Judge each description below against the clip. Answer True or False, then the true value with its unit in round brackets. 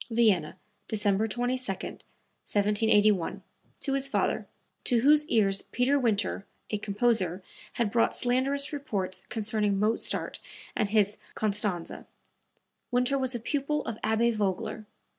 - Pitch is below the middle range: False (220 Hz)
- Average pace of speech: False (120 wpm)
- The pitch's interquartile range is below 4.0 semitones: True (3.4 semitones)